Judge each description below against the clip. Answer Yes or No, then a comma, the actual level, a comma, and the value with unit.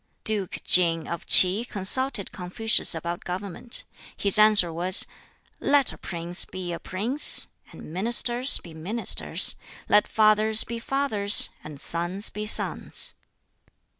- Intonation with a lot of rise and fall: No, average, 4.1 semitones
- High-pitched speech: Yes, high, 200 Hz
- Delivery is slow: Yes, slow, 125 wpm